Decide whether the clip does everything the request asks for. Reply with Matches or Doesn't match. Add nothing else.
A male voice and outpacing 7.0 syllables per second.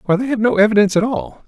Matches